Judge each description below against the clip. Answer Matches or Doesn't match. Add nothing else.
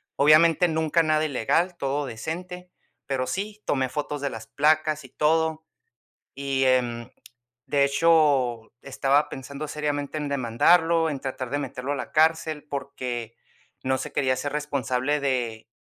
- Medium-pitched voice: Matches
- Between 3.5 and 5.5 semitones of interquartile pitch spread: Doesn't match